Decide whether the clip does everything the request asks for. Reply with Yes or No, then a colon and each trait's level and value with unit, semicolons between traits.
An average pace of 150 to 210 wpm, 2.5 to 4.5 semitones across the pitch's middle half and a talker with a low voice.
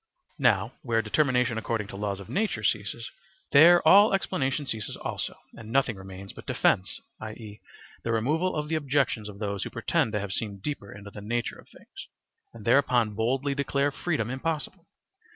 No: average, 170 wpm; wide, 5.4 semitones; low, 120 Hz